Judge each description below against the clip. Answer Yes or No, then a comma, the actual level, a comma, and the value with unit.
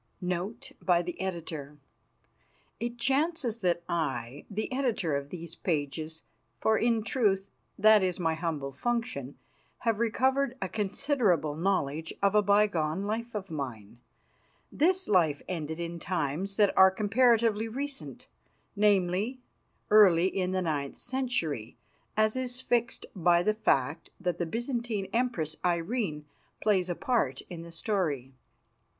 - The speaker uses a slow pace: Yes, slow, 130 wpm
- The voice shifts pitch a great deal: Yes, wide, 5.9 semitones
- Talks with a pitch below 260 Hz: Yes, high, 190 Hz